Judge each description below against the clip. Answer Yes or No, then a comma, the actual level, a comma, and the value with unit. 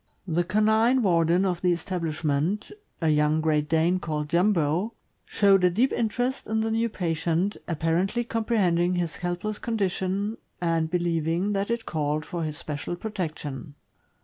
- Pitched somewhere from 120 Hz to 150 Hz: No, medium, 175 Hz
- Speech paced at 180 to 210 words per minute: No, average, 150 wpm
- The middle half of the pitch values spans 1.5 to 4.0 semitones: No, average, 4.4 semitones